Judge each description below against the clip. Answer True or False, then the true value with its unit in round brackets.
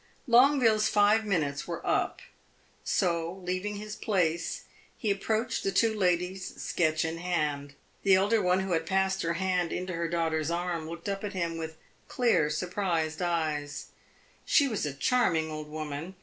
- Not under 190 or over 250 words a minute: False (160 wpm)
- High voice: False (180 Hz)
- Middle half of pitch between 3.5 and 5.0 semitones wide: True (3.8 semitones)